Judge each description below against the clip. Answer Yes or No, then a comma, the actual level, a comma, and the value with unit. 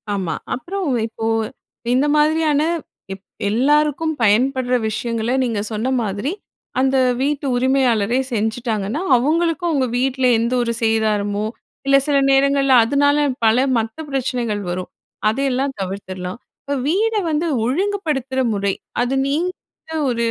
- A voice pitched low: No, very high, 255 Hz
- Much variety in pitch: No, average, 4.5 semitones